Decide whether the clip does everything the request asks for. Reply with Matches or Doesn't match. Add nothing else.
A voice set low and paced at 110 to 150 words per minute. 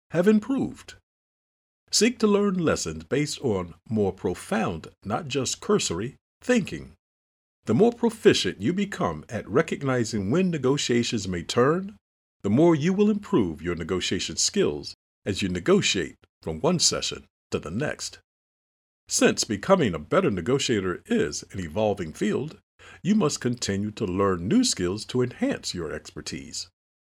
Matches